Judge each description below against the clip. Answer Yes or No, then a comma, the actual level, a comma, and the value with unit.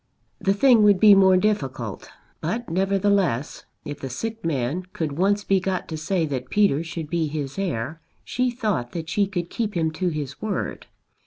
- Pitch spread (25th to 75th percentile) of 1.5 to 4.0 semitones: No, average, 5.0 semitones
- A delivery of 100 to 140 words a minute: No, average, 180 wpm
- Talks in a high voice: No, medium, 175 Hz